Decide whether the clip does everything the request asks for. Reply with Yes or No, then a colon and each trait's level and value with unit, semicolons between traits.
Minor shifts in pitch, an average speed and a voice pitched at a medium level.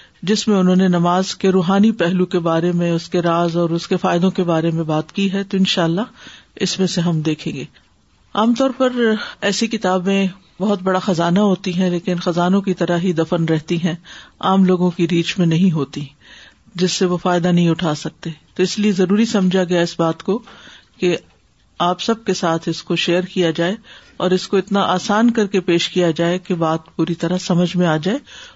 No: narrow, 2.1 semitones; fast, 215 wpm; medium, 180 Hz